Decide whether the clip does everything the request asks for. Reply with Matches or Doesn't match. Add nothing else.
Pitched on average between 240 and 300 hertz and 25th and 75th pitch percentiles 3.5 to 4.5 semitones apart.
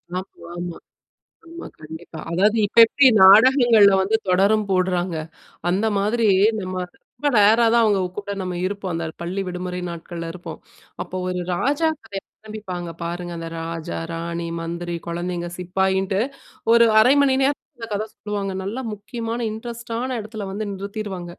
Doesn't match